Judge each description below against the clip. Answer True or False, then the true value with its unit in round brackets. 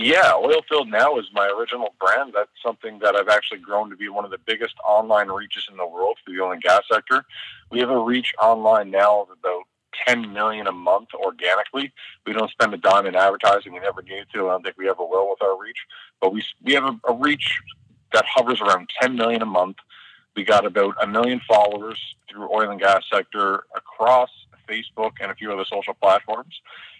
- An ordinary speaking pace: False (215 wpm)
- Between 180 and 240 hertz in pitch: False (110 Hz)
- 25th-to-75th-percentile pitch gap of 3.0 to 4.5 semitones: True (3.6 semitones)